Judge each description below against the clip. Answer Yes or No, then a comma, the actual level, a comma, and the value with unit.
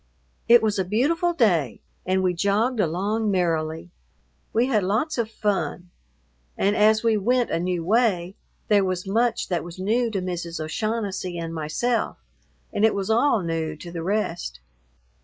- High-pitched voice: Yes, high, 195 Hz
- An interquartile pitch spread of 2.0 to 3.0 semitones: No, average, 4.4 semitones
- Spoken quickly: No, average, 160 wpm